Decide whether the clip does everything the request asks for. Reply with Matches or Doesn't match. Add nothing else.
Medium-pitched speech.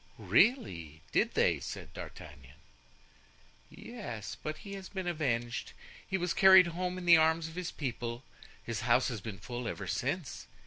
Matches